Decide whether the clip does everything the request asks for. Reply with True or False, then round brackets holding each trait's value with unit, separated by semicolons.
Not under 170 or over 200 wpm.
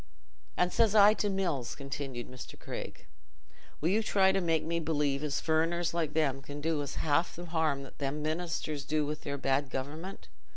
True (180 wpm)